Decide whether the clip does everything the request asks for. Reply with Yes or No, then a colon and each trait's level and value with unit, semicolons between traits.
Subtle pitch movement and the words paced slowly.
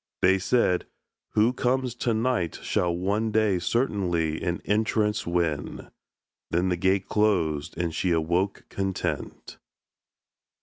No: average, 4.0 semitones; slow, 120 wpm